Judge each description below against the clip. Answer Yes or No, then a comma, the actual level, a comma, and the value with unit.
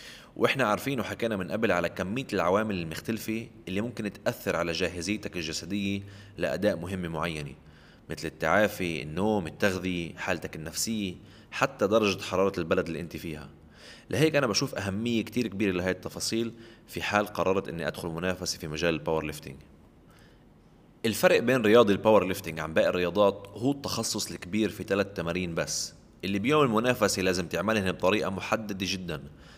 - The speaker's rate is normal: No, fast, 145 wpm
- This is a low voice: Yes, low, 100 Hz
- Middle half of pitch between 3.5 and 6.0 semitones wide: Yes, average, 4.0 semitones